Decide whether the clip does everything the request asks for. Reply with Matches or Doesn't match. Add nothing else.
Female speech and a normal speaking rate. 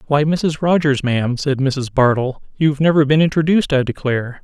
Doesn't match